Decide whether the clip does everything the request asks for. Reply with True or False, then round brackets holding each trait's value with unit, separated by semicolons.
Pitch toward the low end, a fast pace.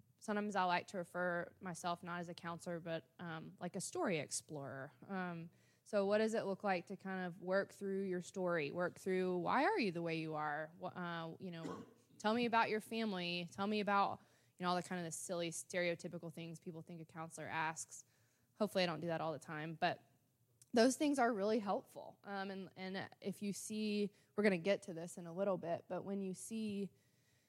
False (180 Hz; 215 wpm)